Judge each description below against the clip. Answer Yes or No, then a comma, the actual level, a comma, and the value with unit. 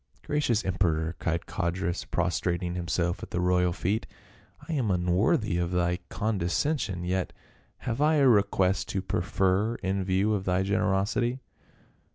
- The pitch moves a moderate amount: Yes, average, 3.3 semitones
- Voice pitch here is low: Yes, very low, 95 Hz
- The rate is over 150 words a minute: Yes, average, 160 wpm